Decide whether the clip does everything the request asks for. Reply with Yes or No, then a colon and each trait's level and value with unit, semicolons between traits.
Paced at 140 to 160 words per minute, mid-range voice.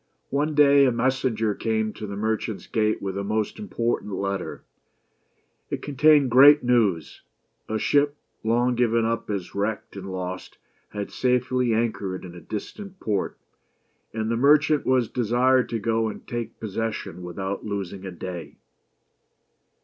No: average, 150 wpm; low, 115 Hz